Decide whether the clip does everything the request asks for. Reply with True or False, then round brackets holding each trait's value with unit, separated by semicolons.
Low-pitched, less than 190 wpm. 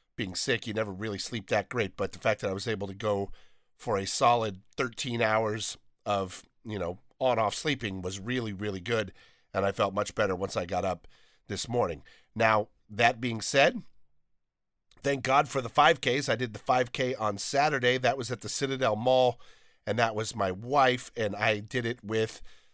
False (110 Hz; 195 wpm)